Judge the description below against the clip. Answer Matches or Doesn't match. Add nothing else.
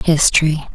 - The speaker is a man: Doesn't match